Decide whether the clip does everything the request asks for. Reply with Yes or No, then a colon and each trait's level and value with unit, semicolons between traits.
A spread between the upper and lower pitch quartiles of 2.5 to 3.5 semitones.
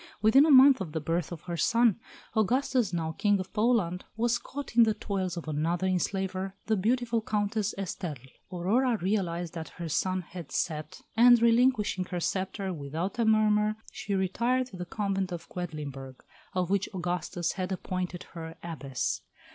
No: average, 4.2 semitones